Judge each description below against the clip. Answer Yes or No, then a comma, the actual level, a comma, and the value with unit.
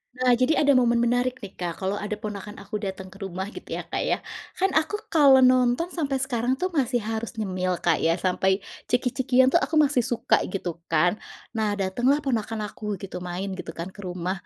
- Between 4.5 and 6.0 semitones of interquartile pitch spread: Yes, average, 5.1 semitones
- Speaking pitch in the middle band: No, high, 225 Hz